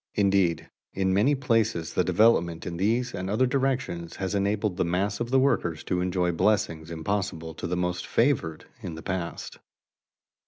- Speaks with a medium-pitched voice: No, very low, 95 Hz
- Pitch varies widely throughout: No, average, 4.3 semitones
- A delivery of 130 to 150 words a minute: No, average, 165 wpm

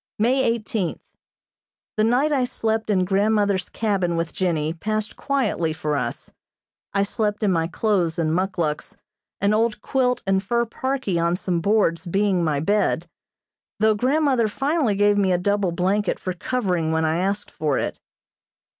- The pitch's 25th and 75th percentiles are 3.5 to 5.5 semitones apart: Yes, average, 4.2 semitones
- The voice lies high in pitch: Yes, high, 200 Hz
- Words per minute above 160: No, average, 155 wpm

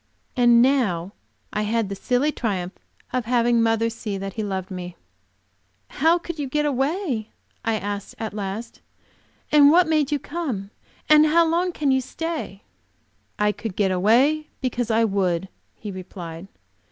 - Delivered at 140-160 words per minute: Yes, average, 155 wpm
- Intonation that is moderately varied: No, wide, 6.6 semitones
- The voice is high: Yes, high, 230 Hz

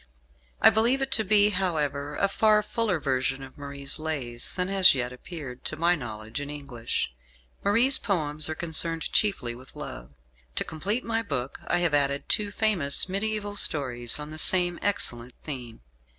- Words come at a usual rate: Yes, average, 165 wpm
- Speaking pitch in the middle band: Yes, medium, 155 Hz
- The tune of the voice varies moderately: No, wide, 6.7 semitones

